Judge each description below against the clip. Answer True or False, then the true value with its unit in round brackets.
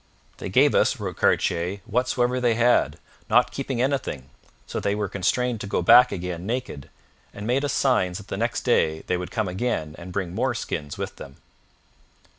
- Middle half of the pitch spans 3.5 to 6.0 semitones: True (5.6 semitones)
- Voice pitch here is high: False (105 Hz)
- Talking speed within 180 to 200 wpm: True (190 wpm)